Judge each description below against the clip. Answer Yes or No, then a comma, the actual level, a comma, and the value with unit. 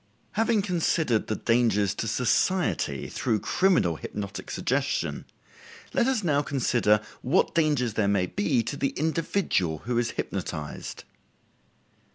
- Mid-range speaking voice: No, low, 120 Hz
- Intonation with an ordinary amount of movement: No, wide, 7.9 semitones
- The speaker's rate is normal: No, slow, 125 wpm